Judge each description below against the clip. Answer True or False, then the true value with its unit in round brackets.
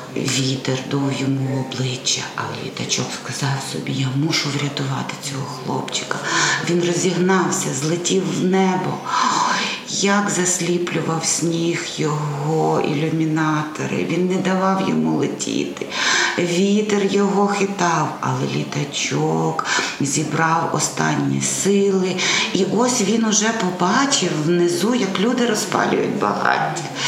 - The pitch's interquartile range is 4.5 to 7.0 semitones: True (5.5 semitones)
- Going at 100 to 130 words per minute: True (105 wpm)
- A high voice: False (170 Hz)